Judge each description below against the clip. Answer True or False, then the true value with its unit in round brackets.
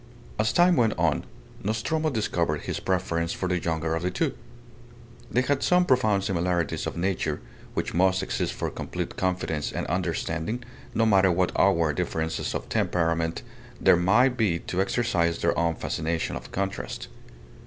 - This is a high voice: False (90 Hz)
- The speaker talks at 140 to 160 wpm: True (155 wpm)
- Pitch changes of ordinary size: True (4.5 semitones)